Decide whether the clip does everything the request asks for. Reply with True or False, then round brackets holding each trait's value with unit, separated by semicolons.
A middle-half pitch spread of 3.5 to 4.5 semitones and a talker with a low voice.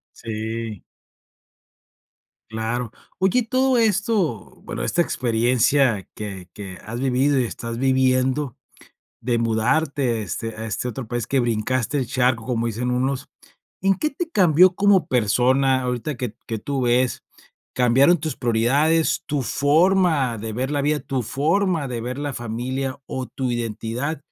True (3.9 semitones; 130 Hz)